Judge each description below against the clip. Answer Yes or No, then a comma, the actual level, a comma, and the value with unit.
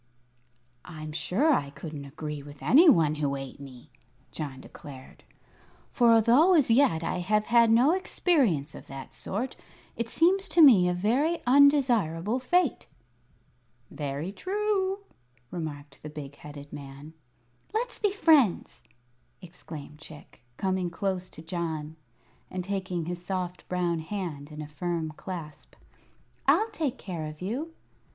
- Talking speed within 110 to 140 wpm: Yes, slow, 135 wpm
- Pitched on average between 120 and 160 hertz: No, medium, 180 Hz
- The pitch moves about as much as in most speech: No, wide, 8.7 semitones